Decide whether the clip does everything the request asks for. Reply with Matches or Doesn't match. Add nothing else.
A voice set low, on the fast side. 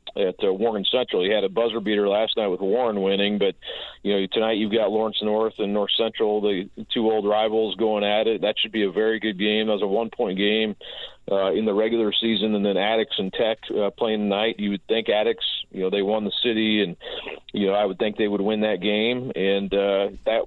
Matches